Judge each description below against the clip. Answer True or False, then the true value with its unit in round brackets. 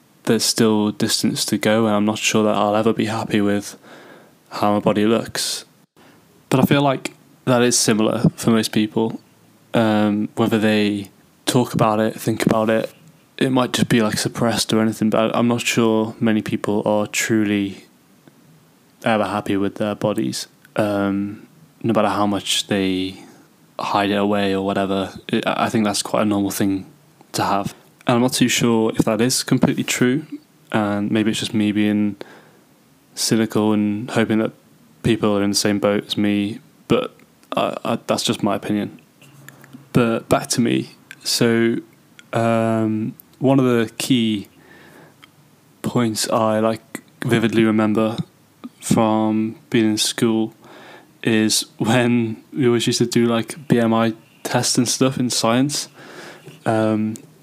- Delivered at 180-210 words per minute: False (155 wpm)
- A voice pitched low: True (110 Hz)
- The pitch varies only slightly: True (2.0 semitones)